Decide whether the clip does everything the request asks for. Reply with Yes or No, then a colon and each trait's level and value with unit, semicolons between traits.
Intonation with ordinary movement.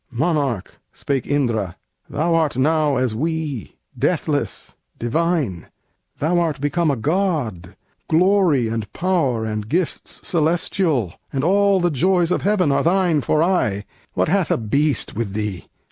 No: wide, 6.8 semitones